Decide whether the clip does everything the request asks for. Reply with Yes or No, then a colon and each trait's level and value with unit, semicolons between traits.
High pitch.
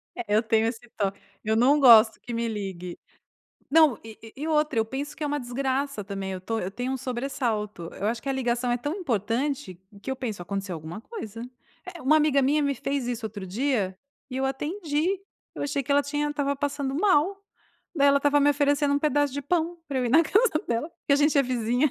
Yes: very high, 265 Hz